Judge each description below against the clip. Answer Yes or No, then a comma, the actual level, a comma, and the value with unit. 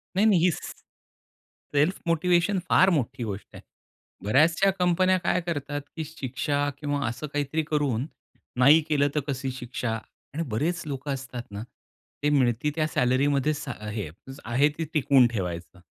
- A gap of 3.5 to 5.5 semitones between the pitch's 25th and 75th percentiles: Yes, average, 4.1 semitones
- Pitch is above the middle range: No, medium, 145 Hz